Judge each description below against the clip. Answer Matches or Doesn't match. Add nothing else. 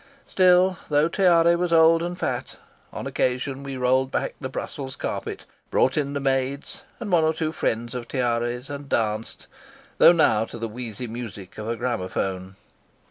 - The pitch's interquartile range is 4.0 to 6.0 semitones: Matches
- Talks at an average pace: Matches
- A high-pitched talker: Doesn't match